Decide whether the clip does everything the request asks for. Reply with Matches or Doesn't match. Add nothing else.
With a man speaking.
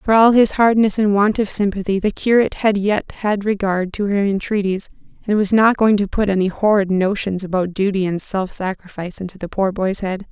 Doesn't match